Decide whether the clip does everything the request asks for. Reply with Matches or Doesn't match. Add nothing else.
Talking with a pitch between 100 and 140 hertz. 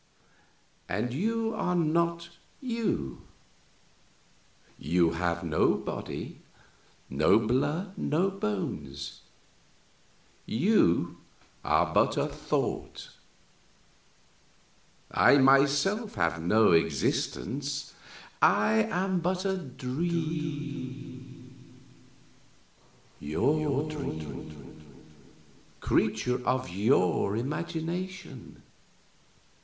Matches